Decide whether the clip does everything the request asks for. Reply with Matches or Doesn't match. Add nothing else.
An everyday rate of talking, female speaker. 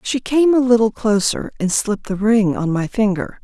Doesn't match